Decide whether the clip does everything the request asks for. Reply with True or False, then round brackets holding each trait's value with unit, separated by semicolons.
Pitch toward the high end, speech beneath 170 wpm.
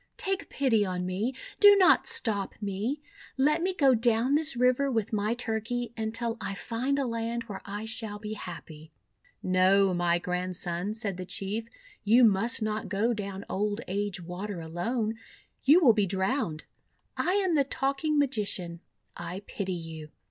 True (215 Hz; 160 wpm)